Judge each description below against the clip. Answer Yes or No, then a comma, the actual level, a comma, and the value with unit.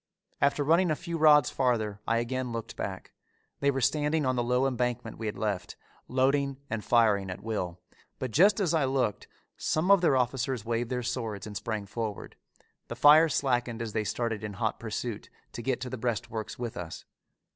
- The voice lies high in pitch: No, low, 120 Hz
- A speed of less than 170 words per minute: No, average, 190 wpm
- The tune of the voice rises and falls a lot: No, average, 3.8 semitones